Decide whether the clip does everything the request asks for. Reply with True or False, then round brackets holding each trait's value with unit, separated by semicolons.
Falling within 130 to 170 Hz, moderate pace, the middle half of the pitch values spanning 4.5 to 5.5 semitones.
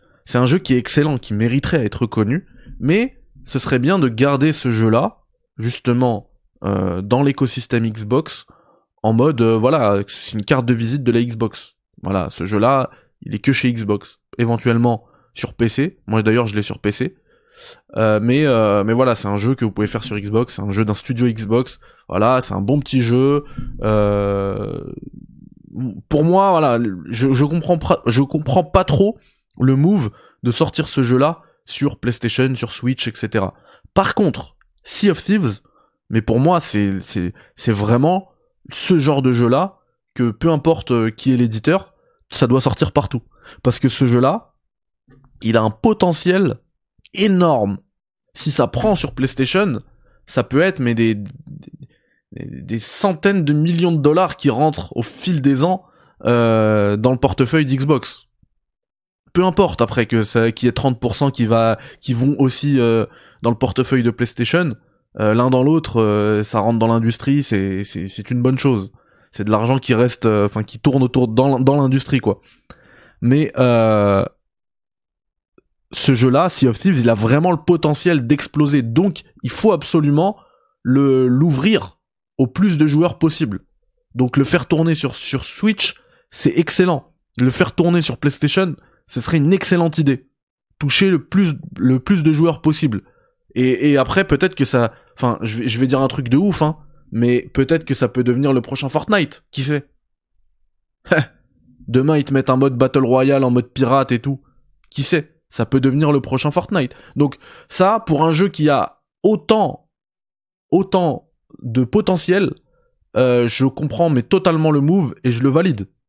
True (135 Hz; 175 wpm; 5.2 semitones)